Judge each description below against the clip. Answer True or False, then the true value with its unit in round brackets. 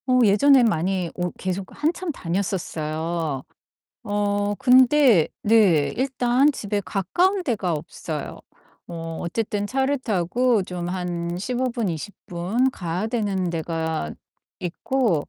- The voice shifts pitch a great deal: True (6.3 semitones)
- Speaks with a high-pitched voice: True (200 Hz)